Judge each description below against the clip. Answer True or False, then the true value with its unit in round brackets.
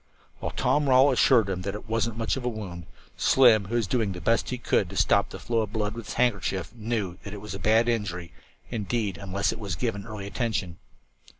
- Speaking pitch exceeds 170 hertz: False (110 Hz)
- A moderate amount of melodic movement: True (3.0 semitones)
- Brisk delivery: True (225 wpm)